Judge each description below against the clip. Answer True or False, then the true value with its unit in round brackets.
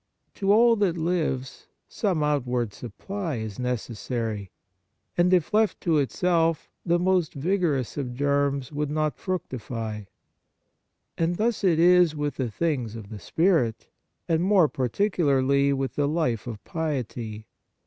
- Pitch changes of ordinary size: False (5.8 semitones)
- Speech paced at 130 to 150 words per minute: True (140 wpm)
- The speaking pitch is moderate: True (150 Hz)